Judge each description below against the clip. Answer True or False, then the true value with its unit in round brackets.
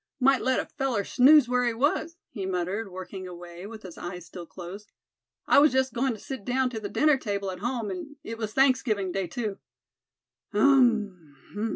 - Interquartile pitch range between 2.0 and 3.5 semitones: False (5.6 semitones)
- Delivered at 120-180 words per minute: False (190 wpm)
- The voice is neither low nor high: False (220 Hz)